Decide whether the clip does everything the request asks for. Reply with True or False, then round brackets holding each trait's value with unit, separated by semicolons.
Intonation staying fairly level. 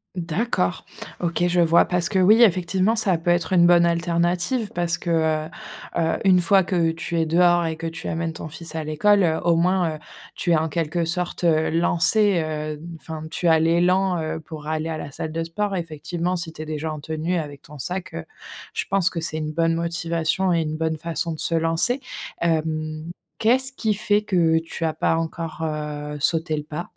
True (2.0 semitones)